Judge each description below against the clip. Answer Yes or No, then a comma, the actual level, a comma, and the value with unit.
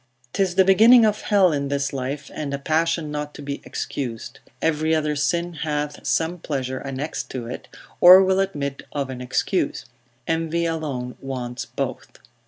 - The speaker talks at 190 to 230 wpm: No, average, 165 wpm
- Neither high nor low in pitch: Yes, medium, 150 Hz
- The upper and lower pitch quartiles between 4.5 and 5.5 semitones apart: No, average, 3.7 semitones